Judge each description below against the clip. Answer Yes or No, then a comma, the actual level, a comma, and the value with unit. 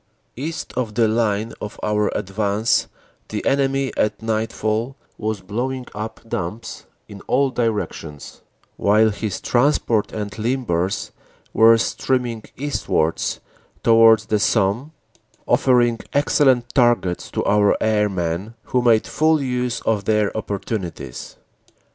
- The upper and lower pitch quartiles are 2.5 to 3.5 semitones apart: Yes, average, 3.1 semitones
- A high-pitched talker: No, low, 110 Hz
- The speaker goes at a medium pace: No, slow, 120 wpm